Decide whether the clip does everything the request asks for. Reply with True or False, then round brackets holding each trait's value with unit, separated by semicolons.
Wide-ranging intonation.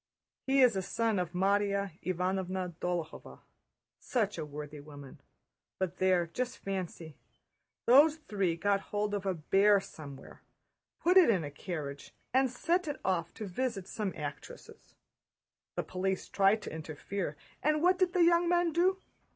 True (6.5 semitones)